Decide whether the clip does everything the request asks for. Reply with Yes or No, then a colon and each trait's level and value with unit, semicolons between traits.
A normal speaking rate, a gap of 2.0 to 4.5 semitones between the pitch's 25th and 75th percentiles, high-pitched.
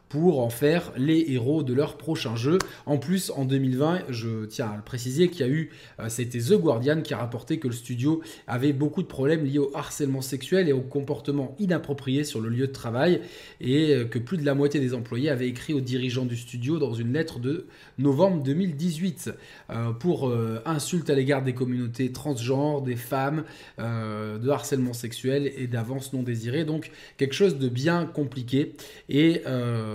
No: average, 190 wpm; average, 3.5 semitones; medium, 140 Hz